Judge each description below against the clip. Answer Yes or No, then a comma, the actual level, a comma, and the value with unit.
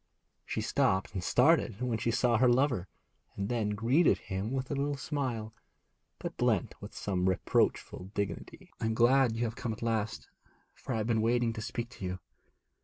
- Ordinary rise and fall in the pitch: Yes, average, 3.2 semitones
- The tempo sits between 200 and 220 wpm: No, average, 185 wpm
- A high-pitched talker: No, low, 115 Hz